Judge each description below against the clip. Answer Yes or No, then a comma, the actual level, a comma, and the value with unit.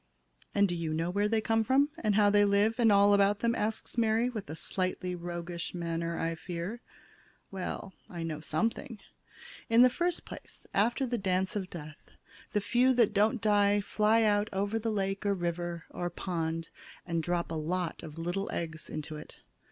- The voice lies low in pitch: No, high, 195 Hz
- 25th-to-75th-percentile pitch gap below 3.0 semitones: No, average, 4.1 semitones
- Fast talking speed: No, average, 185 wpm